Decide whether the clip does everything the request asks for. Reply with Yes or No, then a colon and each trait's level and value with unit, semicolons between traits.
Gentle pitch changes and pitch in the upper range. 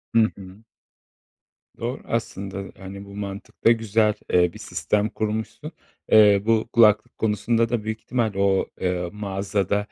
No: narrow, 2.2 semitones; low, 105 Hz